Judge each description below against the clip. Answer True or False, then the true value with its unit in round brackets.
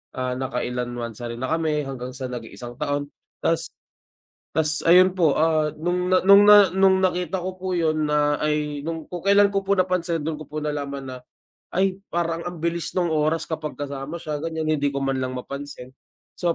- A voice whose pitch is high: False (155 Hz)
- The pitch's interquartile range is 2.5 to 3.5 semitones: False (4.1 semitones)